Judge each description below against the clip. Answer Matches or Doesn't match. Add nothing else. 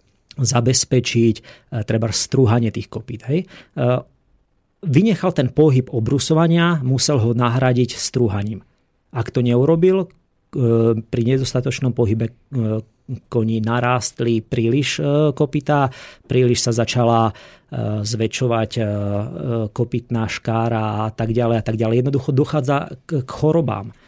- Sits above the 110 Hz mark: Matches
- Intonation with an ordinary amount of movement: Matches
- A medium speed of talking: Doesn't match